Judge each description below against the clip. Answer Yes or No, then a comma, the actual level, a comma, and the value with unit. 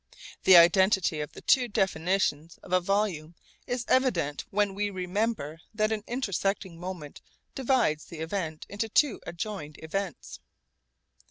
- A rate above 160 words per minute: No, slow, 135 wpm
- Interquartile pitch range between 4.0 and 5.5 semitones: Yes, average, 4.3 semitones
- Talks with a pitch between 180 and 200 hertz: Yes, high, 190 Hz